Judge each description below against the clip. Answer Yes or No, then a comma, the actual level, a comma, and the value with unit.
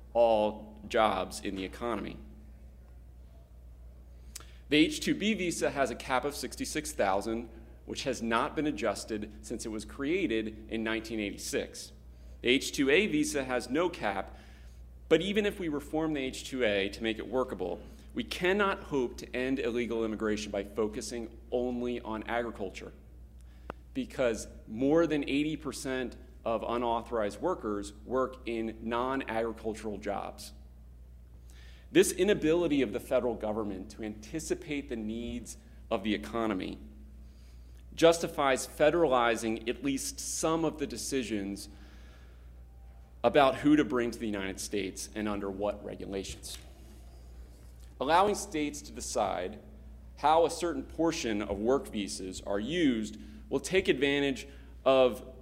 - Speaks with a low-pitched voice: Yes, low, 110 Hz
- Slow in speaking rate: Yes, slow, 130 wpm